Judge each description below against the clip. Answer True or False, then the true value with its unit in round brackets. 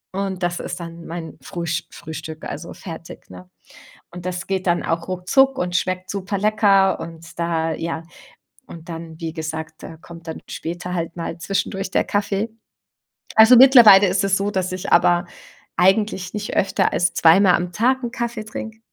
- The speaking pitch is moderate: True (180 Hz)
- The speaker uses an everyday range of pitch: True (3.0 semitones)